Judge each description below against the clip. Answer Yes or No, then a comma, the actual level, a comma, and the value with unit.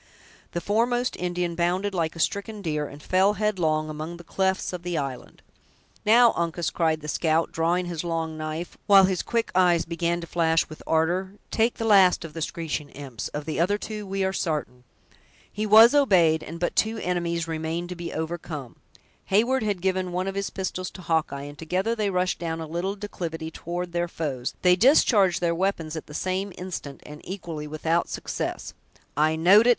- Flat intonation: No, average, 3.2 semitones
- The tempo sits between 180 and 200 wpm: Yes, average, 190 wpm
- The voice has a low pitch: No, medium, 175 Hz